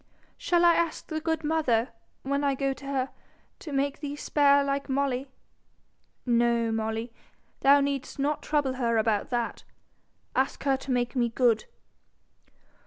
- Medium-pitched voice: No, very high, 275 Hz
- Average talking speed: Yes, average, 150 wpm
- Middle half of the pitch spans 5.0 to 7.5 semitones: No, average, 3.0 semitones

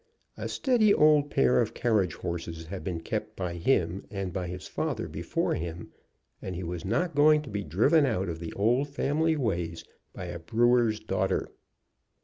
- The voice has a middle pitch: No, very low, 95 Hz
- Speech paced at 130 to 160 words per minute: No, average, 175 wpm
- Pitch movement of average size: No, wide, 8.3 semitones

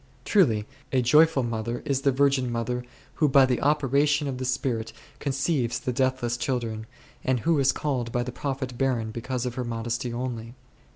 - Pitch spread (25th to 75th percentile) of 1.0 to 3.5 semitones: Yes, narrow, 2.6 semitones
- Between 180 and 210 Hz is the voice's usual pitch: No, low, 125 Hz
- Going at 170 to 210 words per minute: Yes, average, 175 wpm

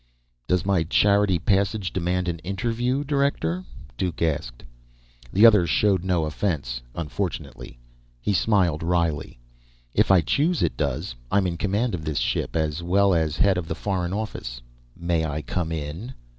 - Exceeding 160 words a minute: No, average, 155 wpm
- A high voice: No, very low, 90 Hz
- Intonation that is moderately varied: Yes, average, 4.0 semitones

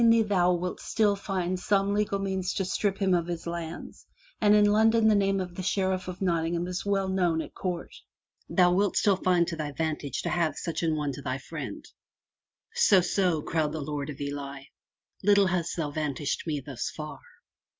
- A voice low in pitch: No, medium, 180 Hz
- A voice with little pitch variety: No, average, 3.8 semitones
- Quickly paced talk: Yes, fast, 210 wpm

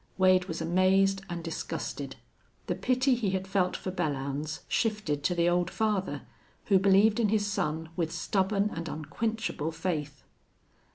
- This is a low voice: No, medium, 185 Hz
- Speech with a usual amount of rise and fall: Yes, average, 3.8 semitones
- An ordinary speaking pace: Yes, average, 150 wpm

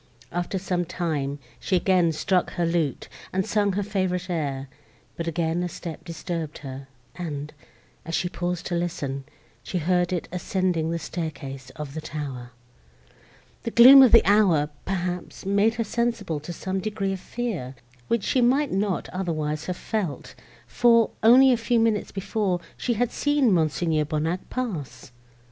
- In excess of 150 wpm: Yes, average, 160 wpm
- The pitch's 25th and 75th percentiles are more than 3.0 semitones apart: Yes, average, 4.6 semitones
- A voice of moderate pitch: Yes, medium, 180 Hz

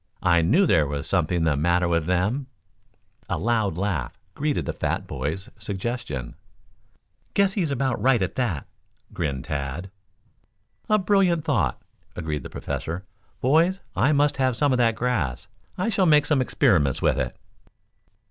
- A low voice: Yes, low, 105 Hz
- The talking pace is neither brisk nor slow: Yes, average, 150 wpm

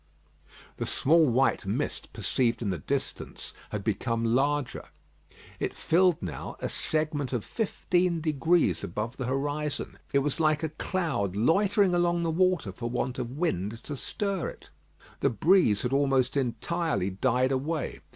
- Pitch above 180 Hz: No, medium, 140 Hz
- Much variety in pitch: Yes, wide, 5.7 semitones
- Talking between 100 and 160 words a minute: Yes, average, 150 wpm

